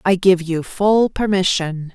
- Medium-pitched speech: Yes, medium, 180 Hz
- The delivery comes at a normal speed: Yes, average, 155 wpm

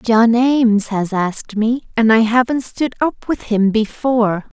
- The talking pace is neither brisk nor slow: Yes, average, 170 wpm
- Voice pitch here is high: Yes, high, 230 Hz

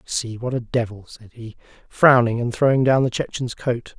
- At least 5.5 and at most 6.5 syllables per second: No, 4.9 syllables/s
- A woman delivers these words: No, male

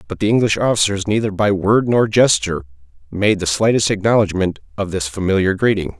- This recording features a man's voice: Yes, male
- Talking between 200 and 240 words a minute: No, average, 170 wpm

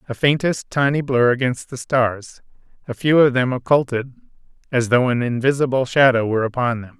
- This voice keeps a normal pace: Yes, average, 170 wpm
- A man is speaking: Yes, male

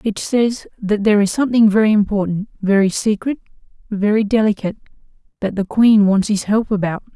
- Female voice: Yes, female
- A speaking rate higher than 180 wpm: No, average, 160 wpm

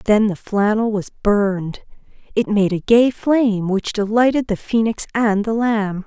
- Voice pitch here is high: Yes, high, 215 Hz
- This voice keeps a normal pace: Yes, average, 170 wpm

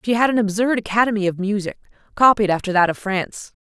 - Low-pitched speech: No, high, 205 Hz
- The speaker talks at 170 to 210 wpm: Yes, average, 200 wpm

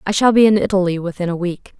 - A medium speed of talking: No, fast, 270 wpm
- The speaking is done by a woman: Yes, female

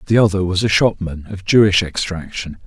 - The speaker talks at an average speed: Yes, average, 180 wpm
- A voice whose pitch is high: No, very low, 95 Hz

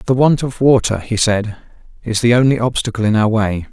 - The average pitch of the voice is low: Yes, low, 115 Hz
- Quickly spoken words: Yes, fast, 210 wpm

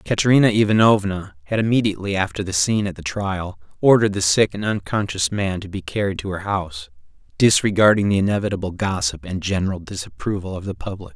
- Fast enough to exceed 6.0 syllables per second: Yes, 6.2 syllables/s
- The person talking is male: Yes, male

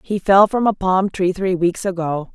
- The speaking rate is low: No, fast, 230 wpm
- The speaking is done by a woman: Yes, female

